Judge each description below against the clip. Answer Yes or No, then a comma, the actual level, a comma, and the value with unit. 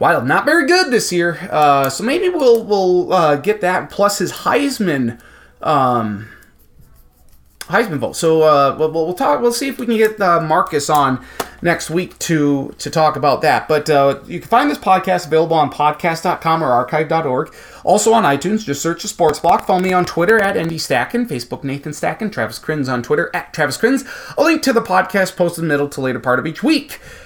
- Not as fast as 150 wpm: No, fast, 205 wpm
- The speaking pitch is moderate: Yes, medium, 170 Hz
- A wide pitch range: Yes, wide, 6.2 semitones